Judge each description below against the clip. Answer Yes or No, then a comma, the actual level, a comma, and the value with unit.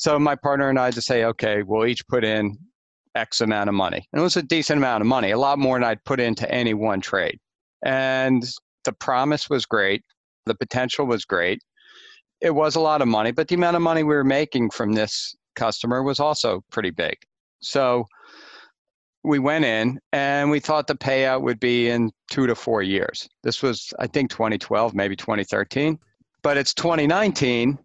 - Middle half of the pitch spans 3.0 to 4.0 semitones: No, average, 4.5 semitones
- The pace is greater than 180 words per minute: Yes, average, 195 wpm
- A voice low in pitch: Yes, low, 130 Hz